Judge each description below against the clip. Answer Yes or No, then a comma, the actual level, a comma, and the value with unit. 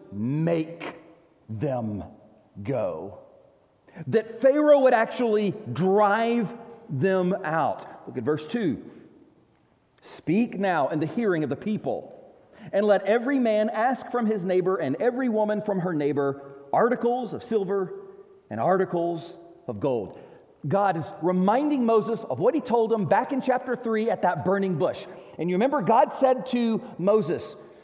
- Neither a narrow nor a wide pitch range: No, wide, 5.8 semitones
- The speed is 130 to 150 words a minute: Yes, average, 145 wpm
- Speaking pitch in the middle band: No, high, 205 Hz